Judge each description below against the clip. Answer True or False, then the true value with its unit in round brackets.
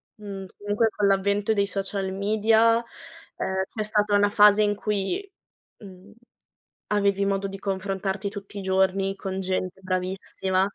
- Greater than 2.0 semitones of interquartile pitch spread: False (1.4 semitones)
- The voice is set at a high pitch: True (200 Hz)